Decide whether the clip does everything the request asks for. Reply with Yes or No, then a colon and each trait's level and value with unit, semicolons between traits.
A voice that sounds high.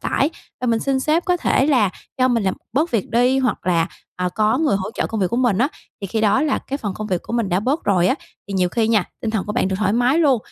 Yes: high, 230 Hz